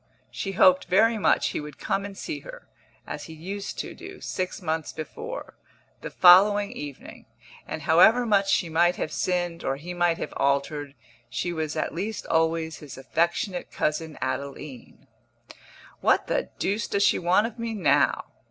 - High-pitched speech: No, medium, 175 Hz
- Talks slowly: No, average, 165 wpm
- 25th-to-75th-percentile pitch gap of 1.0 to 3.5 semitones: No, average, 4.2 semitones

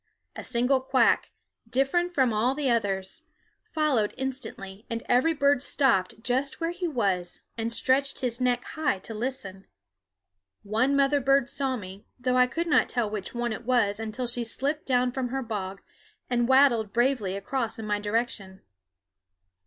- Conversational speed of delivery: Yes, average, 160 wpm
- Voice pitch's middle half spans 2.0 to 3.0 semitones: No, average, 3.9 semitones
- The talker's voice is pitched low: No, high, 245 Hz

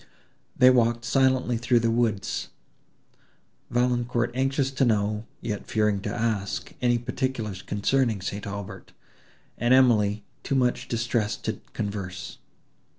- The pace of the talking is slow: Yes, slow, 120 wpm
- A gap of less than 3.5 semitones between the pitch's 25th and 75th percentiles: Yes, average, 3.1 semitones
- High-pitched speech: No, low, 115 Hz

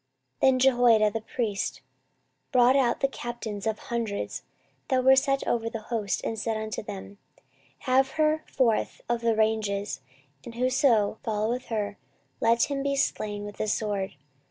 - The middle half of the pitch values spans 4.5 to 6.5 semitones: No, average, 3.2 semitones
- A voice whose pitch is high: Yes, high, 230 Hz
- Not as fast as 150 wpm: No, average, 155 wpm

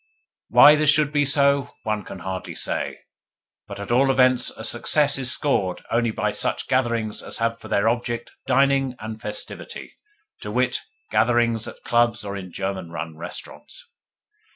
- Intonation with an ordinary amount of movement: Yes, average, 4.2 semitones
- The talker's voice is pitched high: No, low, 120 Hz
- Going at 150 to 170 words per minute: Yes, average, 160 wpm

